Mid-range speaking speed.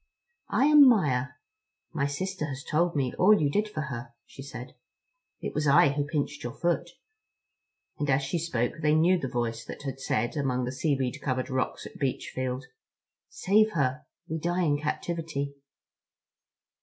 Yes: average, 165 wpm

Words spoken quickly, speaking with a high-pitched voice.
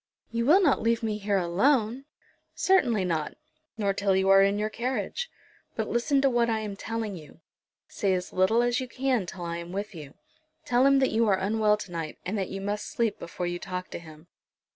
Yes: fast, 215 wpm; high, 210 Hz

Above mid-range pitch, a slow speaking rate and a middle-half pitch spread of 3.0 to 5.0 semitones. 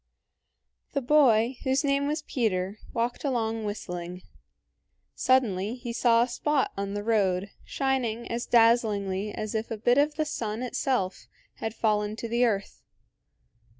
No: high, 230 Hz; average, 145 wpm; average, 3.5 semitones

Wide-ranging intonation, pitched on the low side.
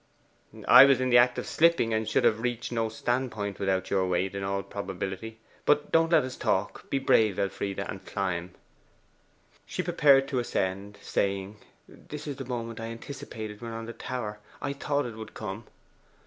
No: average, 4.5 semitones; low, 115 Hz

